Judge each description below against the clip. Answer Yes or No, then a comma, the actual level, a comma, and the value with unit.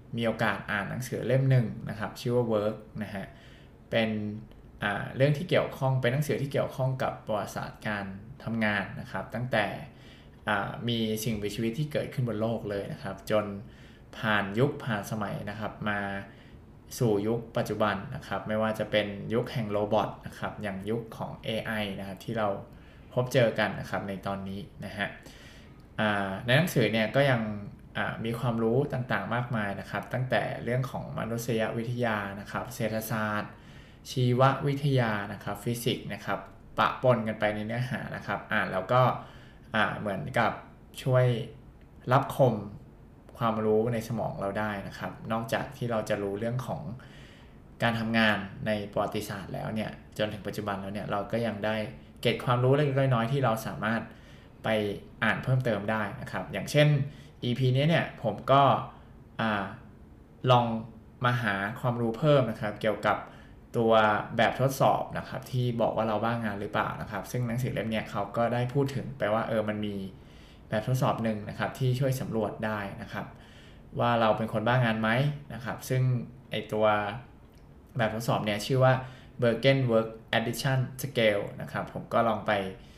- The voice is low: Yes, low, 115 Hz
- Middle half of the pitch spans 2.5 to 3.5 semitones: Yes, average, 3.1 semitones